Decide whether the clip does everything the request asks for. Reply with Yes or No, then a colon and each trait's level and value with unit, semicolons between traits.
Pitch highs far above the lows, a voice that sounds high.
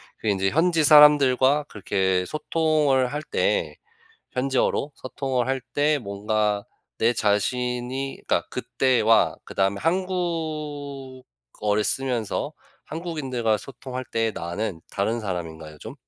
No: wide, 5.9 semitones; low, 125 Hz